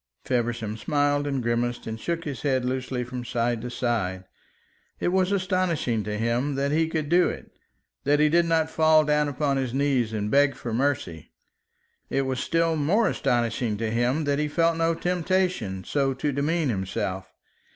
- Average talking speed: Yes, average, 175 wpm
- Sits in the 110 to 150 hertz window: Yes, low, 135 Hz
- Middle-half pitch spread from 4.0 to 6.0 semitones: Yes, average, 5.0 semitones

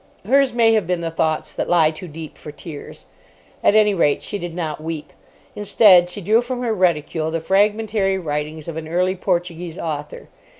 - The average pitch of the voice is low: No, medium, 175 Hz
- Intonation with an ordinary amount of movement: Yes, average, 4.4 semitones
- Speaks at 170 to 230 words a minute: Yes, average, 185 wpm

